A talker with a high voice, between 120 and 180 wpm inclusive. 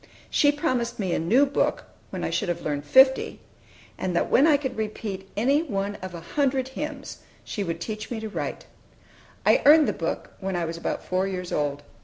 No: high, 215 Hz; fast, 205 wpm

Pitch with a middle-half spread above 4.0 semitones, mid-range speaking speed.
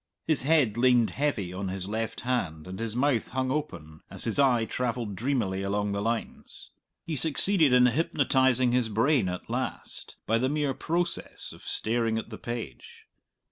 Yes: average, 4.5 semitones; average, 170 wpm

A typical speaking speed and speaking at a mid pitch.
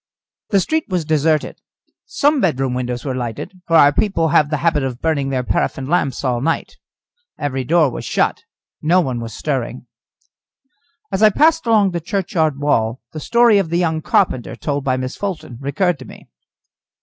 Yes: average, 175 wpm; medium, 155 Hz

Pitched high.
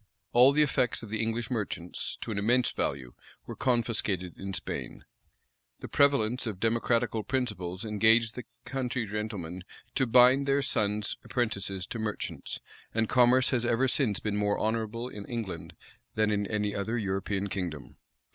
No: low, 110 Hz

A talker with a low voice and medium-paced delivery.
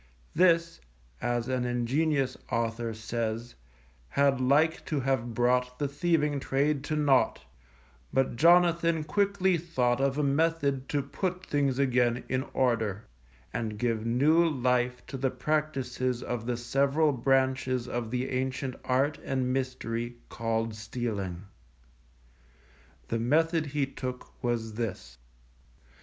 No: low, 130 Hz; slow, 125 wpm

